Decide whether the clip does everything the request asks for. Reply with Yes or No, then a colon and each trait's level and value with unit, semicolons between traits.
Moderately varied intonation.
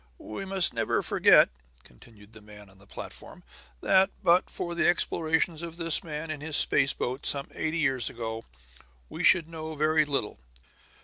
No: wide, 6.2 semitones